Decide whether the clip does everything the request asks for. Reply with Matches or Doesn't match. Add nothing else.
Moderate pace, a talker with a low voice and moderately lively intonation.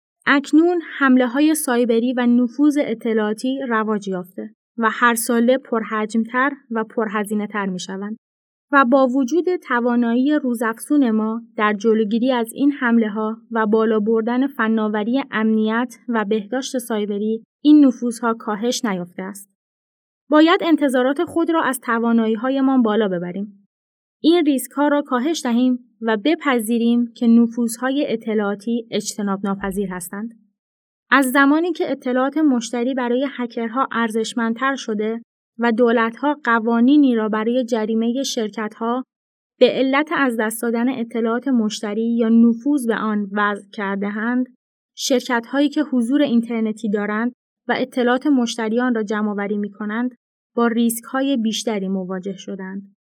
Doesn't match